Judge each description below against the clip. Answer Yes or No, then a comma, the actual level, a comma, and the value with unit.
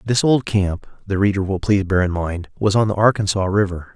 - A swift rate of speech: Yes, fast, 225 wpm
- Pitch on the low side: Yes, low, 100 Hz